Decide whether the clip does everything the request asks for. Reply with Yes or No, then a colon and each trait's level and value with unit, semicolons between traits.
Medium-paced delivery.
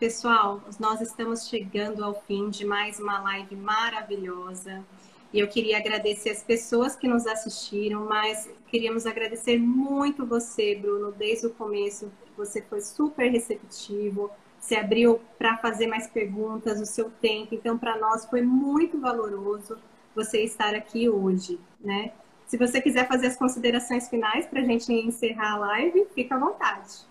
Yes: average, 155 wpm